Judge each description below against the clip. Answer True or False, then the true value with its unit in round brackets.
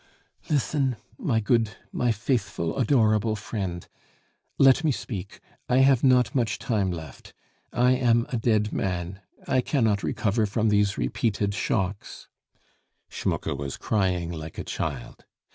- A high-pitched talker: False (110 Hz)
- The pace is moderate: False (130 wpm)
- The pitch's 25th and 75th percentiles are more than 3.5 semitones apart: True (4.2 semitones)